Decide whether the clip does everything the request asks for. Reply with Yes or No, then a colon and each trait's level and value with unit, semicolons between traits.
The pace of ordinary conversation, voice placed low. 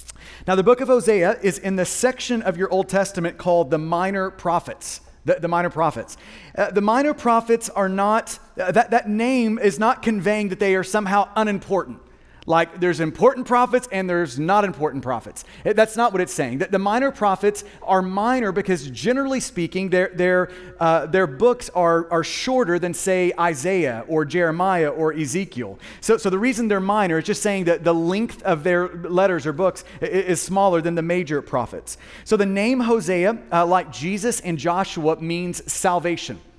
No: average, 180 wpm; high, 190 Hz